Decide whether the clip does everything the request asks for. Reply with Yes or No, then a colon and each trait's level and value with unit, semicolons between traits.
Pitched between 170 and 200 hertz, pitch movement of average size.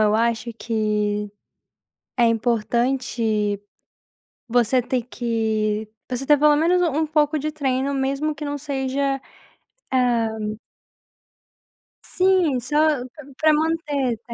No: very high, 255 Hz; average, 4.4 semitones